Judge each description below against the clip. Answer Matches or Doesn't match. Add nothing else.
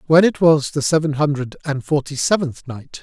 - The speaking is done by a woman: Doesn't match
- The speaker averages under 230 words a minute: Matches